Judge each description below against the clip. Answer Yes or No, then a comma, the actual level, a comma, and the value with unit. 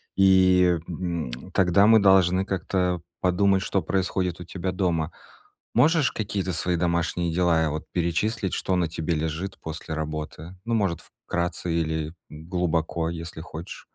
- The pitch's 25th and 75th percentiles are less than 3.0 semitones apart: Yes, narrow, 2.5 semitones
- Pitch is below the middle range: Yes, very low, 90 Hz